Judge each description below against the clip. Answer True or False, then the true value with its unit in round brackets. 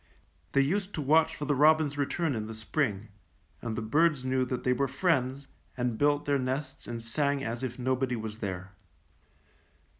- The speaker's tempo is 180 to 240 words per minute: True (185 wpm)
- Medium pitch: False (130 Hz)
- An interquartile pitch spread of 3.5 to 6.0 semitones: True (3.9 semitones)